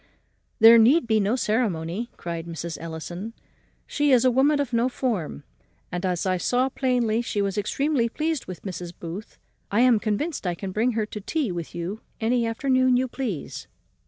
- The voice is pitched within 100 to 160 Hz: No, high, 225 Hz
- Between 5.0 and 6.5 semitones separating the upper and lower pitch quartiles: Yes, wide, 5.6 semitones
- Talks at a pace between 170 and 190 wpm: Yes, average, 185 wpm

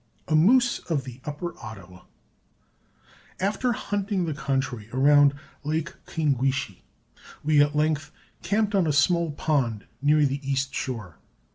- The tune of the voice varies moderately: Yes, average, 4.0 semitones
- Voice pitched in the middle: Yes, medium, 145 Hz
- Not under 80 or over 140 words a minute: Yes, slow, 135 wpm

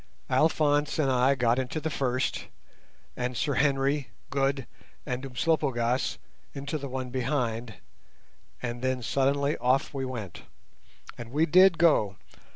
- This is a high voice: No, low, 135 Hz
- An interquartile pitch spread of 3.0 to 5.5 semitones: No, narrow, 2.6 semitones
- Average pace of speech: No, slow, 130 wpm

